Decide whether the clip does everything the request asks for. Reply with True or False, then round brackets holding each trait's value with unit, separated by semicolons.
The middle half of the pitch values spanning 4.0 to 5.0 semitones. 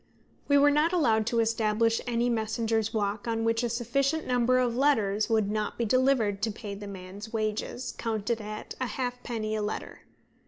False (2.5 semitones)